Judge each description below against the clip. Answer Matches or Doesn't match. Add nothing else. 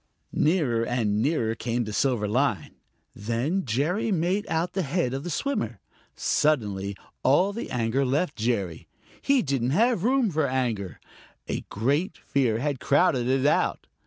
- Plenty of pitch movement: Matches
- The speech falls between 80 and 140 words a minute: Doesn't match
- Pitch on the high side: Doesn't match